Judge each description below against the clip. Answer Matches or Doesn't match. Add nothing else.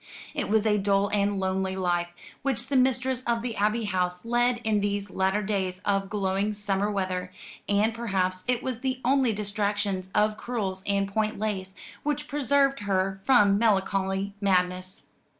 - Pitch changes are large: Doesn't match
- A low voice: Doesn't match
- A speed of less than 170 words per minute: Matches